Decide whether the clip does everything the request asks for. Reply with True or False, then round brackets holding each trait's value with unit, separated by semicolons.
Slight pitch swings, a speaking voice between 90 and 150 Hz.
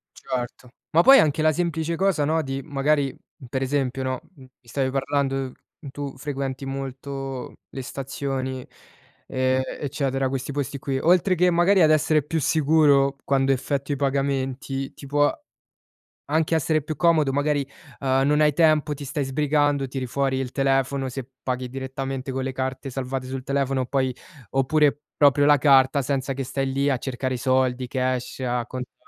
True (1.8 semitones; 135 Hz)